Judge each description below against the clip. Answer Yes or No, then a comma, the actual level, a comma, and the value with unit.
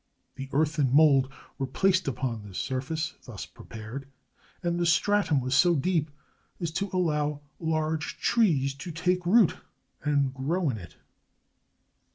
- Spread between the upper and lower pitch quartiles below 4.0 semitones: No, average, 4.3 semitones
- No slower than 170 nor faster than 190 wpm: No, average, 145 wpm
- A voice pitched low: No, medium, 150 Hz